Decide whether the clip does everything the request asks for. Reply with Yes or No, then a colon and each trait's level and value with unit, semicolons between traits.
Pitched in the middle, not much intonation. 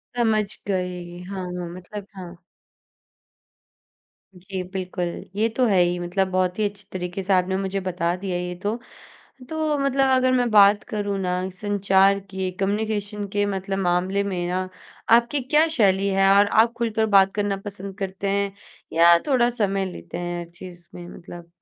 No: high, 195 Hz; narrow, 2.3 semitones